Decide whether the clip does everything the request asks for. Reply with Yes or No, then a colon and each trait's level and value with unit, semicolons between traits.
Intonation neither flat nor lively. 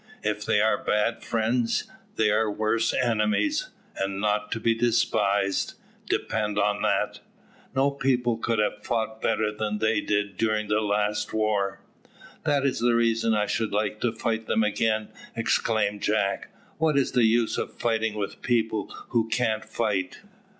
No: narrow, 1.7 semitones